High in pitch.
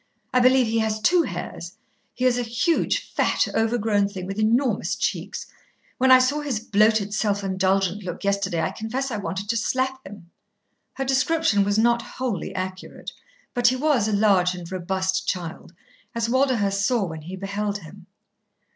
Yes: high, 215 Hz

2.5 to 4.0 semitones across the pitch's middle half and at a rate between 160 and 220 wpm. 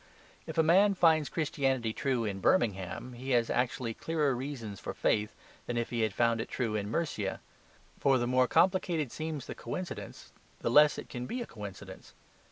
No: average, 5.2 semitones; average, 180 wpm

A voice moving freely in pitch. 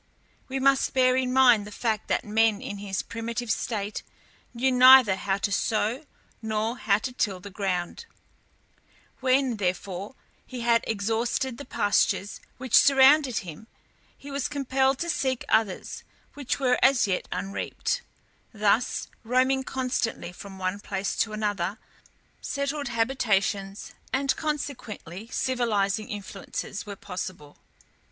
No: average, 4.5 semitones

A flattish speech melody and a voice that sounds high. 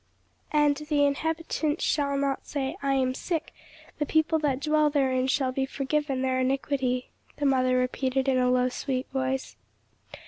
Yes: narrow, 2.3 semitones; very high, 275 Hz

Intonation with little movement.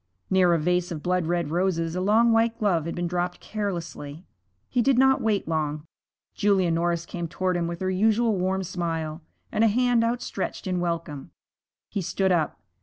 No: average, 3.6 semitones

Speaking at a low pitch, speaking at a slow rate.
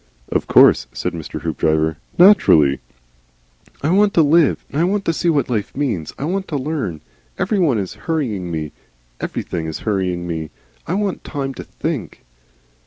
No: low, 130 Hz; average, 165 wpm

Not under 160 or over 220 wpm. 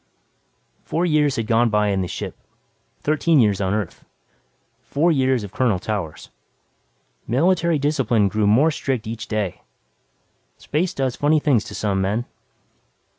No: average, 140 wpm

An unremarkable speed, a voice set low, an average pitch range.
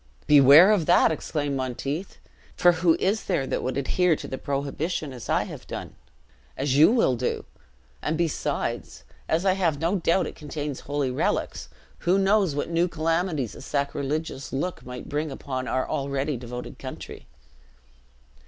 No: average, 160 wpm; medium, 150 Hz; average, 4.0 semitones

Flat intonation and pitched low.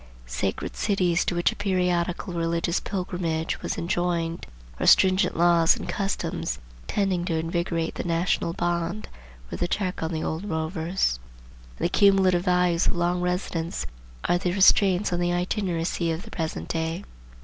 No: narrow, 1.7 semitones; medium, 175 Hz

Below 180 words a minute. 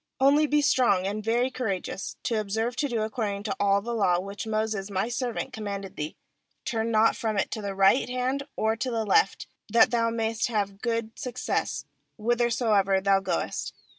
No: average, 185 wpm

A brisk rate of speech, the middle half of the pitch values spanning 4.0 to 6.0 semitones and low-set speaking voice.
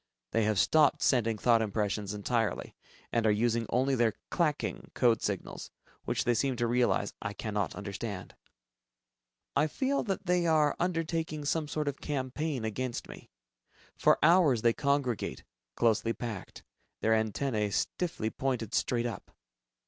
No: average, 140 wpm; average, 5.1 semitones; low, 120 Hz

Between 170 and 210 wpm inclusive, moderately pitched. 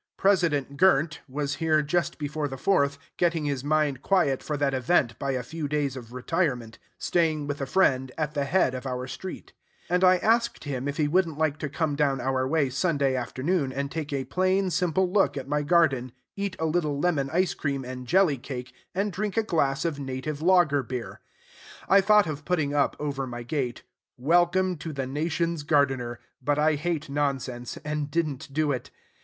Yes: average, 195 wpm; medium, 145 Hz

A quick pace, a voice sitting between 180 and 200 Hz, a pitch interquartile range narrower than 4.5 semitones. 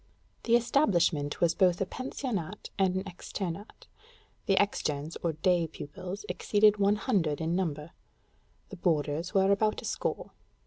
No: average, 140 wpm; medium, 185 Hz; average, 3.9 semitones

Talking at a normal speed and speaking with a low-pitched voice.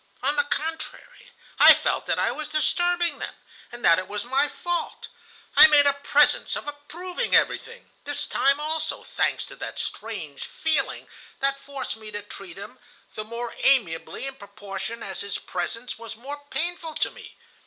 No: average, 170 wpm; very high, 275 Hz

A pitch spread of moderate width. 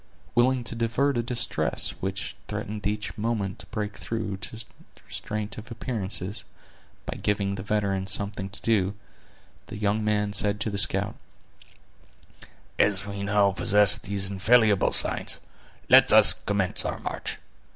No: narrow, 1.9 semitones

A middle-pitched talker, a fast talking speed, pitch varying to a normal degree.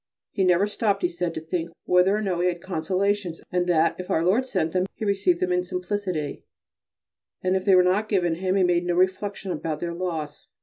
No: medium, 180 Hz; fast, 215 wpm; narrow, 2.1 semitones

